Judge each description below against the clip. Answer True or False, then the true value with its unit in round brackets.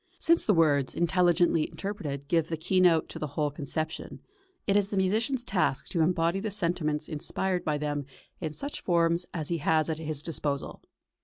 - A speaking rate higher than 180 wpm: False (175 wpm)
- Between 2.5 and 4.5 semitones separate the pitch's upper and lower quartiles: True (3.3 semitones)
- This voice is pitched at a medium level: True (165 Hz)